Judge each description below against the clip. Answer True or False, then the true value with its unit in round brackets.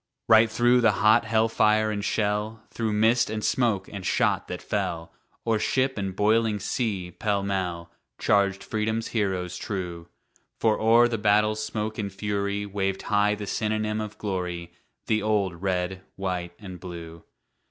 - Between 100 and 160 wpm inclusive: True (155 wpm)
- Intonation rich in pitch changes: False (2.4 semitones)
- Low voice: True (105 Hz)